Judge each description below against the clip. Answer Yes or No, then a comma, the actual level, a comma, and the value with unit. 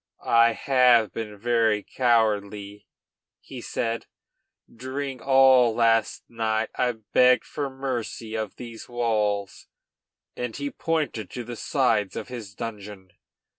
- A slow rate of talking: Yes, slow, 120 wpm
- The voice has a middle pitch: No, low, 115 Hz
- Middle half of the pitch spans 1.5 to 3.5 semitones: Yes, average, 2.7 semitones